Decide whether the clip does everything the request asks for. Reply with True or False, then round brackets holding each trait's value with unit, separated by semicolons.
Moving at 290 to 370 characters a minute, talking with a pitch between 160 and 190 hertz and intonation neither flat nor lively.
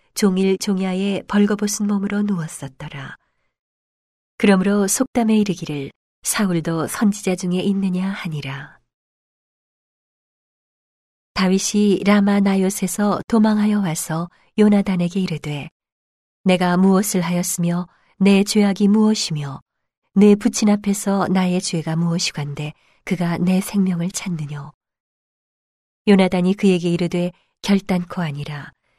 False (255 characters per minute; 185 Hz; 3.0 semitones)